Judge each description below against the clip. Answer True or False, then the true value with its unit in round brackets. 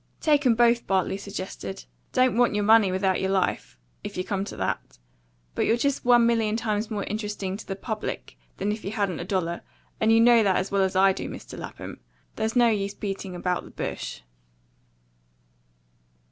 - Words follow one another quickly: False (190 wpm)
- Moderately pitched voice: False (205 Hz)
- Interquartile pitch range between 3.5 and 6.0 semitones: False (3.0 semitones)